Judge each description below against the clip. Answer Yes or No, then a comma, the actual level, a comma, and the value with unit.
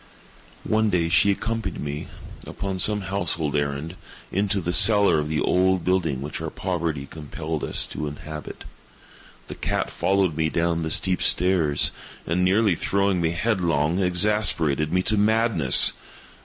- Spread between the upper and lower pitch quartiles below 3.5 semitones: No, average, 3.9 semitones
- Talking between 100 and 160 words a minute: Yes, average, 145 wpm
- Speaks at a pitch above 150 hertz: No, very low, 90 Hz